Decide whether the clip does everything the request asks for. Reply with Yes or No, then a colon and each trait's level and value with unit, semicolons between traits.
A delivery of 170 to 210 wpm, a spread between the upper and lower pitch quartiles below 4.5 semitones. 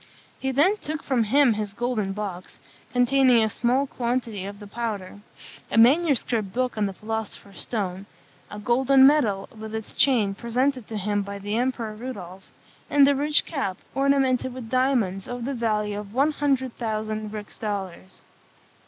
No: average, 160 wpm; average, 4.1 semitones